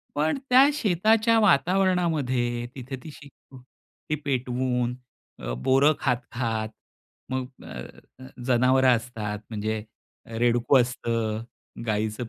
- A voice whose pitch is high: No, low, 125 Hz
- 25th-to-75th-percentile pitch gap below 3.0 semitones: No, average, 3.9 semitones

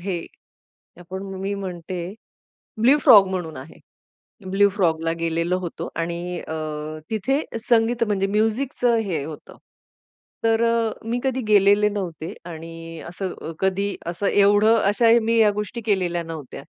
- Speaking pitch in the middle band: No, high, 195 Hz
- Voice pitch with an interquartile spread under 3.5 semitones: No, average, 4.4 semitones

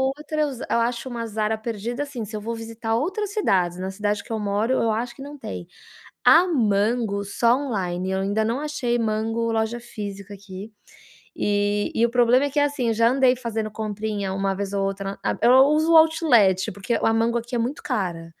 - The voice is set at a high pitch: Yes, high, 225 Hz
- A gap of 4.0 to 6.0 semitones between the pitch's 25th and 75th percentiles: No, average, 3.5 semitones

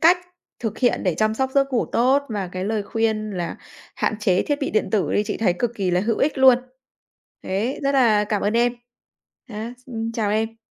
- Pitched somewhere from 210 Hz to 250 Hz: Yes, high, 220 Hz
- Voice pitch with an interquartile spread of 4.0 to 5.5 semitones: No, average, 3.2 semitones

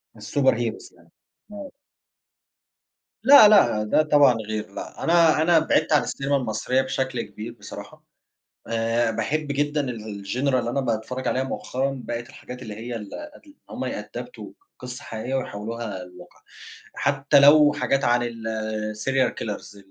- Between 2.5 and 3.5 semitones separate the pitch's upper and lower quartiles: No, average, 4.2 semitones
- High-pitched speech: No, low, 125 Hz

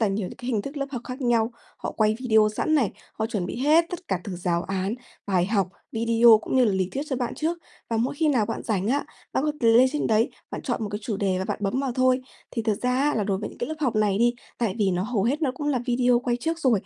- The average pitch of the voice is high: Yes, high, 230 Hz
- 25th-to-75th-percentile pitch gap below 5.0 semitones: Yes, average, 4.1 semitones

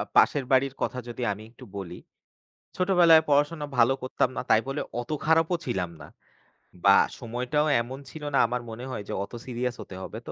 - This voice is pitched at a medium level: No, low, 125 Hz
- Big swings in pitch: No, average, 4.2 semitones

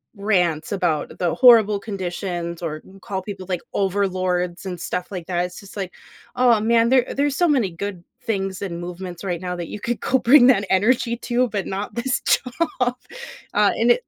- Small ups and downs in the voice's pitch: No, average, 4.7 semitones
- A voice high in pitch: Yes, high, 195 Hz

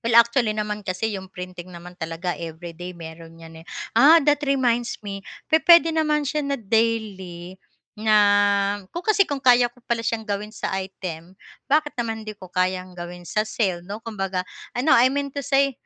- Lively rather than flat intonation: Yes, wide, 5.7 semitones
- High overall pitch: Yes, high, 215 Hz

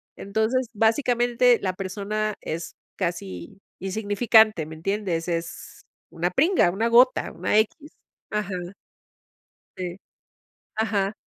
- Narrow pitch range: No, average, 3.8 semitones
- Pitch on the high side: Yes, high, 205 Hz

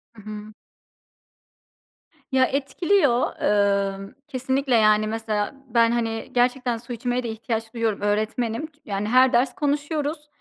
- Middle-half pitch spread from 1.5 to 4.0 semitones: Yes, average, 3.4 semitones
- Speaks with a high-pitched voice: Yes, high, 235 Hz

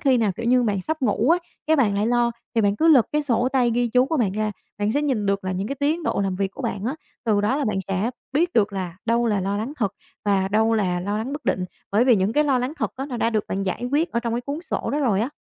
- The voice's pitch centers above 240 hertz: No, high, 230 Hz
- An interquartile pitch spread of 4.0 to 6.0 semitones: Yes, average, 4.7 semitones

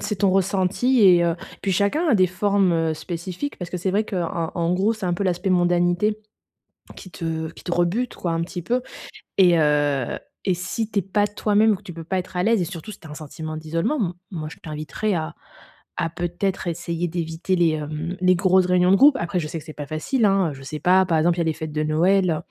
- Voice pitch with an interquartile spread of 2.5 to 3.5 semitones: Yes, average, 3.0 semitones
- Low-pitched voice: No, medium, 175 Hz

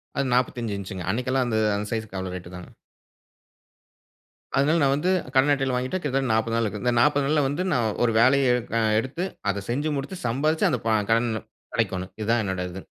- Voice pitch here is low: Yes, low, 125 Hz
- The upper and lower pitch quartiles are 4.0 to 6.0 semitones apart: Yes, average, 4.4 semitones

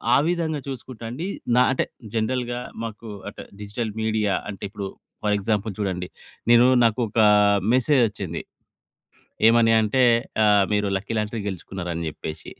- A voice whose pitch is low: Yes, low, 110 Hz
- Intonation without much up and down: No, average, 3.1 semitones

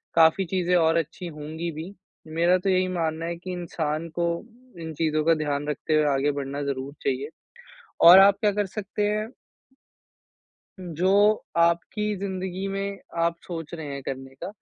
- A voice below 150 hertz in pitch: No, medium, 170 Hz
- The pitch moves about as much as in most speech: Yes, average, 3.5 semitones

